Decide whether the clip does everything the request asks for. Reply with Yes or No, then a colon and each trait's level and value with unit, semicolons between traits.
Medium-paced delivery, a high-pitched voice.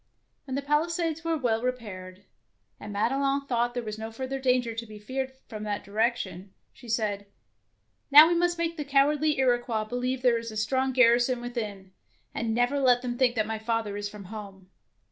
Yes: average, 190 wpm; high, 240 Hz